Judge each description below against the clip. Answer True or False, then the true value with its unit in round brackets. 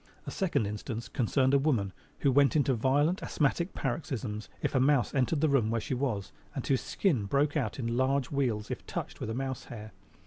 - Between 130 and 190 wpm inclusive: False (200 wpm)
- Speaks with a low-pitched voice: True (130 Hz)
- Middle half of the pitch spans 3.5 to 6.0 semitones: True (3.8 semitones)